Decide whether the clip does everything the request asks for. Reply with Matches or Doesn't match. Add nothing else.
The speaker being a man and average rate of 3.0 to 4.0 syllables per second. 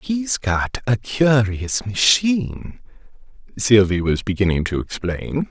Matches